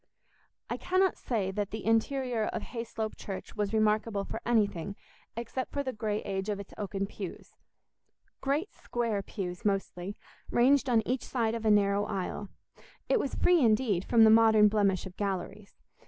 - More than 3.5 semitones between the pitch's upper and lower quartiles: No, average, 3.0 semitones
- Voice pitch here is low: No, high, 215 Hz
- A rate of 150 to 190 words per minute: Yes, average, 160 wpm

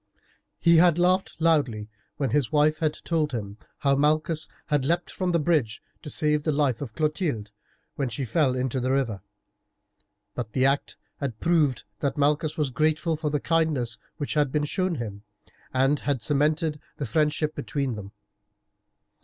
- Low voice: No, medium, 150 Hz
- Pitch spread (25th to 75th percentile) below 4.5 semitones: Yes, average, 3.3 semitones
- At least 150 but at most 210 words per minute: Yes, average, 165 wpm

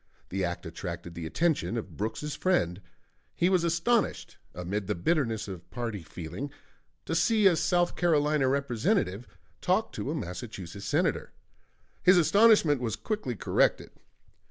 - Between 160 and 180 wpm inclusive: No, slow, 135 wpm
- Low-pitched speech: Yes, low, 130 Hz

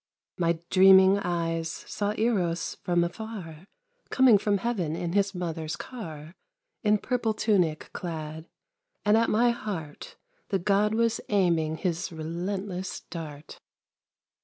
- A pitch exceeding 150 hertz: Yes, medium, 185 Hz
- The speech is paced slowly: Yes, slow, 120 wpm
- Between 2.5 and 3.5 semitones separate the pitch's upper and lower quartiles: No, average, 4.1 semitones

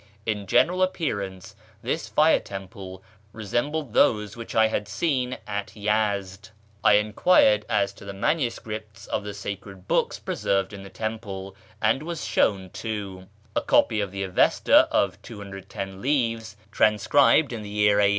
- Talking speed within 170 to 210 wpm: No, average, 150 wpm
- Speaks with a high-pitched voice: No, low, 105 Hz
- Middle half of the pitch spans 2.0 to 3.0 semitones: Yes, narrow, 2.4 semitones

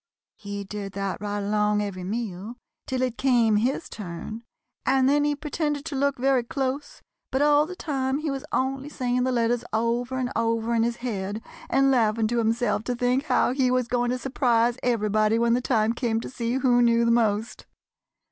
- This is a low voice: No, high, 240 Hz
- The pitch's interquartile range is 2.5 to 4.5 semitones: Yes, average, 3.0 semitones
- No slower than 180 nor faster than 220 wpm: Yes, average, 195 wpm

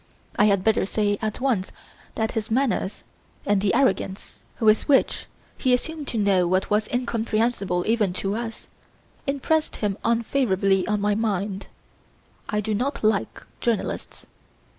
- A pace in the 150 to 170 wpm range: No, average, 140 wpm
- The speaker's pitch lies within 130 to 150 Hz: No, high, 215 Hz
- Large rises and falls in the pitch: No, average, 3.0 semitones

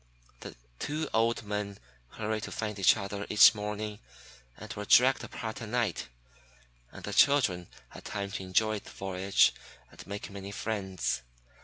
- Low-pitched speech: Yes, low, 105 Hz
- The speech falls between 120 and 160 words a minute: Yes, average, 155 wpm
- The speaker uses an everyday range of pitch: No, narrow, 2.1 semitones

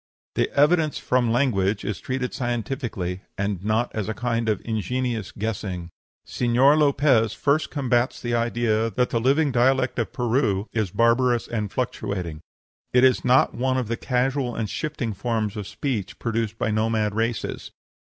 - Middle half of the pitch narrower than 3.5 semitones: Yes, average, 3.0 semitones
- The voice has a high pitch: No, low, 115 Hz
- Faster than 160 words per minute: No, average, 155 wpm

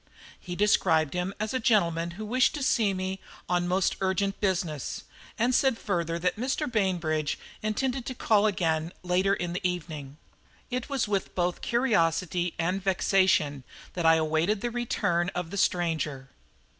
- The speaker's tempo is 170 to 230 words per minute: No, average, 155 wpm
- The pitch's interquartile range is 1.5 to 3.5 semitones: No, average, 4.1 semitones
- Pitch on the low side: No, medium, 185 Hz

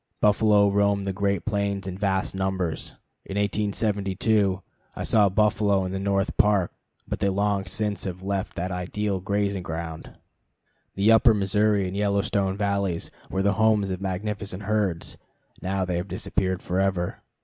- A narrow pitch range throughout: Yes, narrow, 1.4 semitones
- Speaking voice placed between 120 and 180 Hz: No, low, 100 Hz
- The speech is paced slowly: No, average, 150 wpm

